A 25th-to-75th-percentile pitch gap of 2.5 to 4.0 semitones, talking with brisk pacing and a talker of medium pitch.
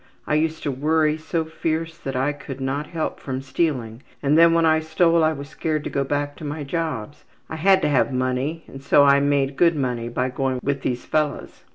Yes: average, 2.9 semitones; fast, 220 wpm; medium, 145 Hz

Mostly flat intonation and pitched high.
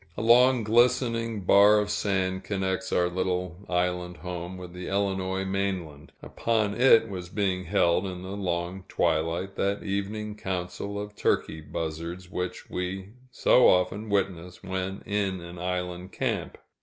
No: narrow, 2.2 semitones; very low, 95 Hz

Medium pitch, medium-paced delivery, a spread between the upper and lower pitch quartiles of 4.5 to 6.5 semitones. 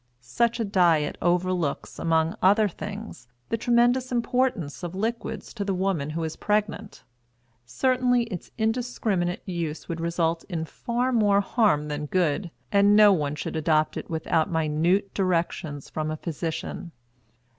Yes: medium, 180 Hz; average, 145 wpm; average, 5.1 semitones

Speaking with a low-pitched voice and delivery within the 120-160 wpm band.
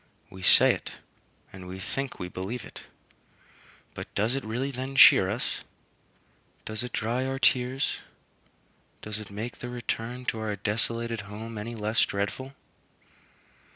Yes: low, 115 Hz; average, 145 wpm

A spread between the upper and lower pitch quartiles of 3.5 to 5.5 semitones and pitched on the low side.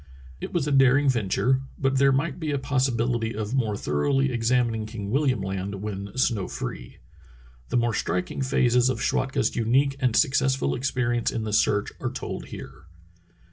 Yes: average, 3.8 semitones; low, 120 Hz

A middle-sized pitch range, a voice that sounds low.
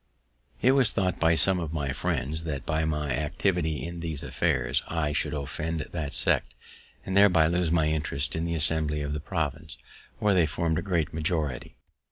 No: narrow, 2.2 semitones; very low, 80 Hz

